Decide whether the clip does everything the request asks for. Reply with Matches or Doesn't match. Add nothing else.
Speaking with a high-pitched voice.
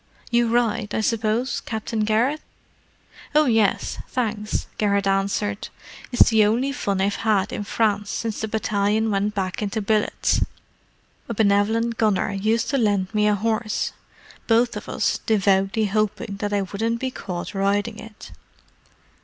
Matches